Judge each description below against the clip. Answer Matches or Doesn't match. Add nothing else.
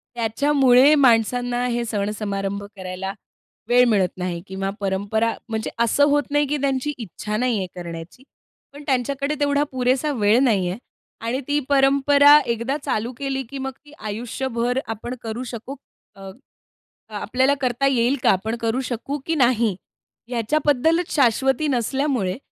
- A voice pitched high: Matches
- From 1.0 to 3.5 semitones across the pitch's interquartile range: Doesn't match